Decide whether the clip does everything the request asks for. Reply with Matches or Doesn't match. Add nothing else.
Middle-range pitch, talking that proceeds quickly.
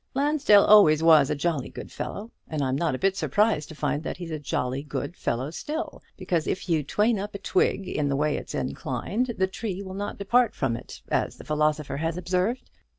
Matches